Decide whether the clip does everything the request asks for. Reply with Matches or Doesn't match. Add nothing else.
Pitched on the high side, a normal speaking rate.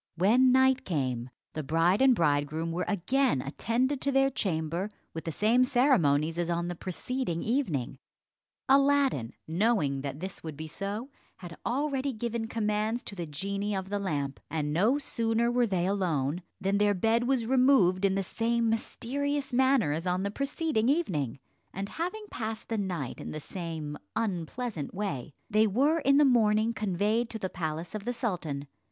Matches